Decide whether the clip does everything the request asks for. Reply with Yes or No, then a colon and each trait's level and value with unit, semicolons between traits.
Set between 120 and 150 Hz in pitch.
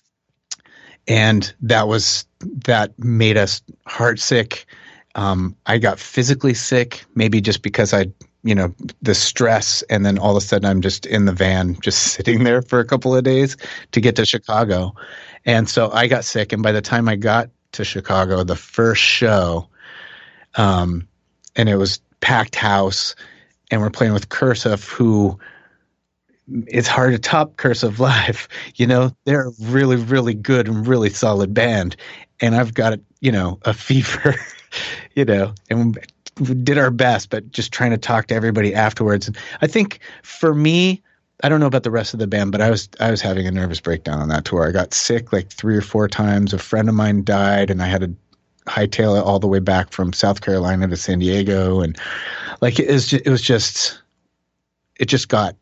No: low, 110 Hz